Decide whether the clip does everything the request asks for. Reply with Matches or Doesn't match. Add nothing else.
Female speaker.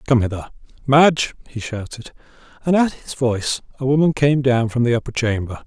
Doesn't match